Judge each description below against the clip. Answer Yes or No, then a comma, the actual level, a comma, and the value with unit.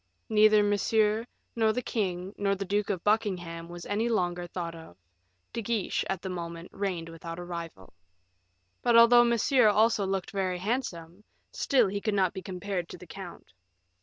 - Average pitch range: Yes, average, 3.6 semitones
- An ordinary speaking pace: Yes, average, 170 wpm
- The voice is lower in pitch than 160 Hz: No, high, 195 Hz